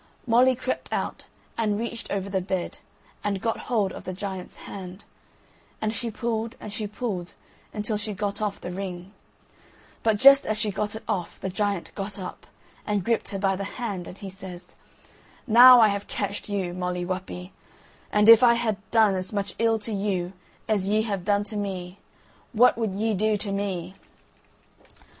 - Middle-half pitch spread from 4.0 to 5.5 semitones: No, narrow, 2.6 semitones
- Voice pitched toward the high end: Yes, high, 205 Hz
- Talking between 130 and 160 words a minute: No, average, 180 wpm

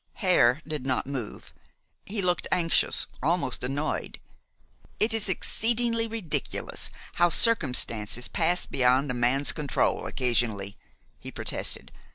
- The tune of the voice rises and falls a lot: Yes, wide, 6.7 semitones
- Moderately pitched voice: Yes, medium, 150 Hz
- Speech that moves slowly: Yes, slow, 115 wpm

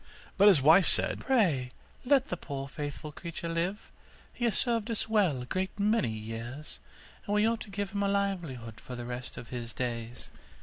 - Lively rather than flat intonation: Yes, wide, 8.4 semitones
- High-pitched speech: No, medium, 170 Hz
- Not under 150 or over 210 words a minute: Yes, average, 190 wpm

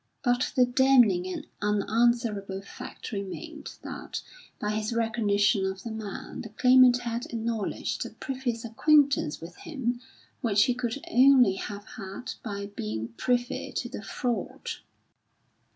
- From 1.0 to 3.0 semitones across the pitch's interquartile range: No, average, 3.5 semitones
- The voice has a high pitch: Yes, high, 225 Hz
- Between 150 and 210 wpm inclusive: No, slow, 135 wpm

